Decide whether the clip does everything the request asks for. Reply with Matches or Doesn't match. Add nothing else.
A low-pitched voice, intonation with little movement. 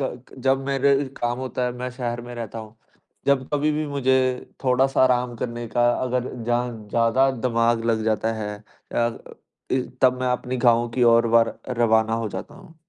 Matches